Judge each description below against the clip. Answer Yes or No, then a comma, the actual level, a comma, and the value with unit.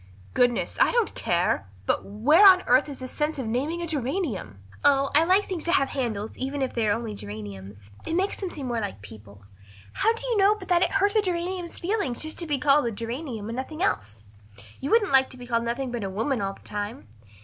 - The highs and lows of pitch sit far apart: Yes, wide, 8.0 semitones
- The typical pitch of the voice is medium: No, very high, 265 Hz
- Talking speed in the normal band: No, fast, 235 wpm